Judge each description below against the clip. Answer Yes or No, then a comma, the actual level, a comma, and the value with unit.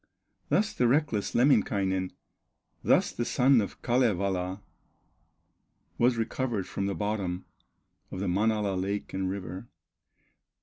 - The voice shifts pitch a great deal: No, average, 3.9 semitones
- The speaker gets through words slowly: Yes, slow, 115 wpm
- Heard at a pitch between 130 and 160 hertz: No, low, 105 Hz